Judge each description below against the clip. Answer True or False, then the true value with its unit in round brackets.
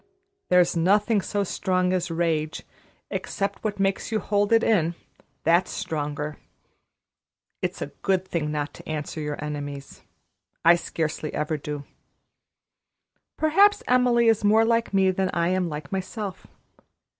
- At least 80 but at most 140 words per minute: True (135 wpm)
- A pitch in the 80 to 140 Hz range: False (180 Hz)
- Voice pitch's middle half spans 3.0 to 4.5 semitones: False (5.0 semitones)